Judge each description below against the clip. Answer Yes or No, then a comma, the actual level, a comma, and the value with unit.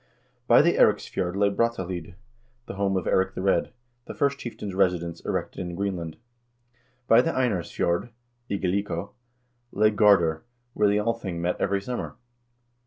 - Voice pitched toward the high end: No, low, 100 Hz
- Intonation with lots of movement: No, average, 3.0 semitones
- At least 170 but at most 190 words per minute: No, average, 140 wpm